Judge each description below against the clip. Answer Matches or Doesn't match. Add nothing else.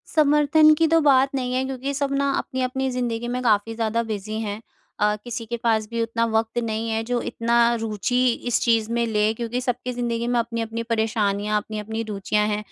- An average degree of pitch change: Doesn't match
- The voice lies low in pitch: Doesn't match